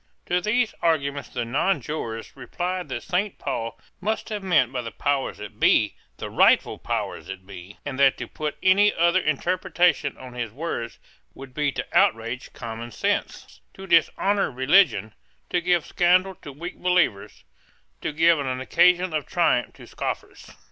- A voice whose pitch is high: No, medium, 155 Hz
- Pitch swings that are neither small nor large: No, wide, 6.3 semitones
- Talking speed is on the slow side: No, average, 160 wpm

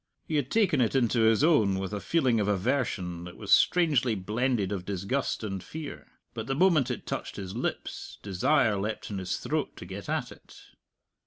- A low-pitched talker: Yes, low, 110 Hz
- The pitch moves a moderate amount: No, wide, 5.7 semitones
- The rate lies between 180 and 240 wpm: Yes, average, 190 wpm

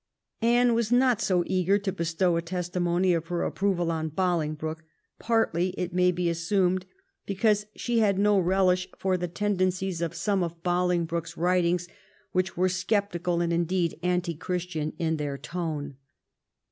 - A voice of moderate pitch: Yes, medium, 180 Hz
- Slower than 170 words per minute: Yes, average, 150 wpm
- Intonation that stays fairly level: Yes, narrow, 2.1 semitones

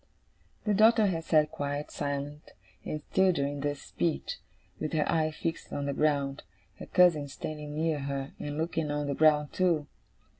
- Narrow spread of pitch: Yes, narrow, 2.2 semitones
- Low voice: No, medium, 150 Hz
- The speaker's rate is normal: Yes, average, 165 wpm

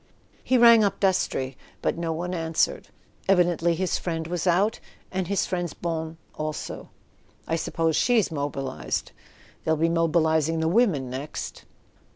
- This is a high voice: No, medium, 165 Hz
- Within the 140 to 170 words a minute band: Yes, average, 145 wpm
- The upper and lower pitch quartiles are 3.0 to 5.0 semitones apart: No, narrow, 2.4 semitones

